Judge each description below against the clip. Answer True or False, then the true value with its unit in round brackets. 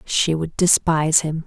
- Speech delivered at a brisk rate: False (165 wpm)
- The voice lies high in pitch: False (160 Hz)